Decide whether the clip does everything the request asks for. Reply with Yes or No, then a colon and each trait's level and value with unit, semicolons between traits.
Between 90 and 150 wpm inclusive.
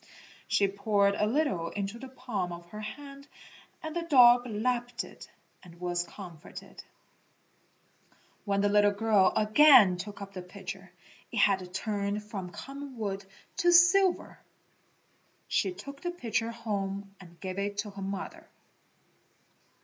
Yes: average, 140 wpm